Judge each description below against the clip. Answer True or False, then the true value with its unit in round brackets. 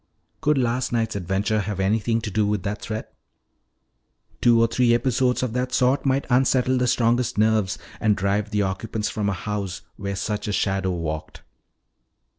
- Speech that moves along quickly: False (175 wpm)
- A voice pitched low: True (110 Hz)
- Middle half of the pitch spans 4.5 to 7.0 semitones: False (3.5 semitones)